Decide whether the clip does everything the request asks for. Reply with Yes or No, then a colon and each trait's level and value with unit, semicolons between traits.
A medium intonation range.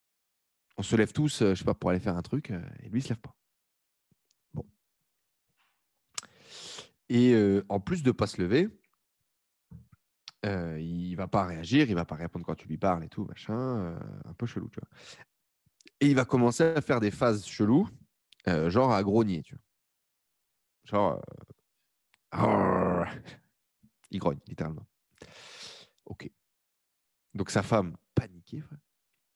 No: wide, 5.9 semitones